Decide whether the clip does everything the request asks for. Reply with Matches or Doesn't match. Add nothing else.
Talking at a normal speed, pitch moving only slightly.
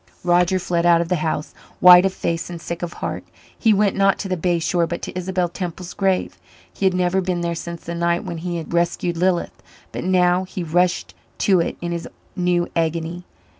Doesn't match